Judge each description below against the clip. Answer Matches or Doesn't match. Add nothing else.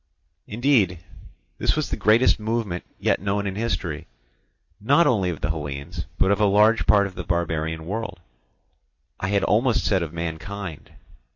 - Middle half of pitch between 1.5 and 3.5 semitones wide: Doesn't match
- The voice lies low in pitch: Matches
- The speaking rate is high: Doesn't match